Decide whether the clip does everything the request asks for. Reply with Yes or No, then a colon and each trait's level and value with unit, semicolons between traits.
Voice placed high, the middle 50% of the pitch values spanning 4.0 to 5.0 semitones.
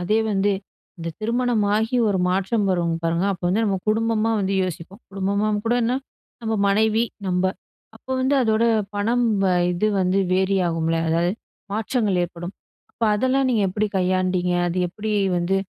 No: high, 200 Hz; average, 3.4 semitones